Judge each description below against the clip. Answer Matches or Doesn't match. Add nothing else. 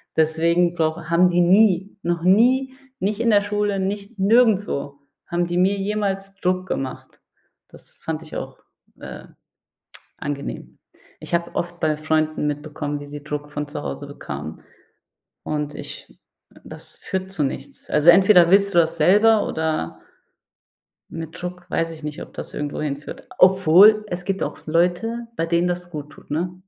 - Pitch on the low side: Doesn't match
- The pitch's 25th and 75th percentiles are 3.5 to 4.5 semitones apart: Matches